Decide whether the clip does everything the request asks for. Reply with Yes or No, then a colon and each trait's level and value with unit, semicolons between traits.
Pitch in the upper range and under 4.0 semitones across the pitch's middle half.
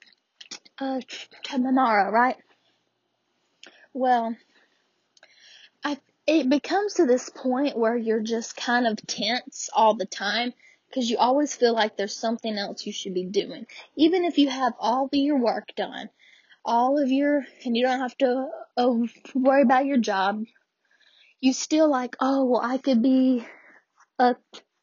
Yes: very high, 255 Hz; average, 3.5 semitones